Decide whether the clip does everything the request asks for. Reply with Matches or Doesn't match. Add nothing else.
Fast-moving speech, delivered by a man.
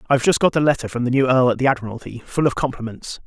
Matches